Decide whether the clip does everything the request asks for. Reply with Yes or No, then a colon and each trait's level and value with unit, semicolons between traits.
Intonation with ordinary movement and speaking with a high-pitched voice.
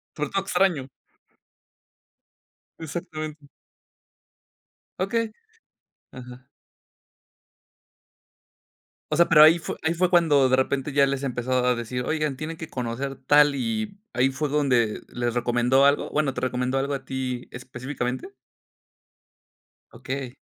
No: average, 3.5 semitones; low, 135 Hz